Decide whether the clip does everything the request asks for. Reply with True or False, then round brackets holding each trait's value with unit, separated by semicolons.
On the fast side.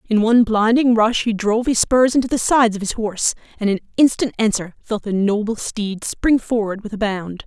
True (215 wpm)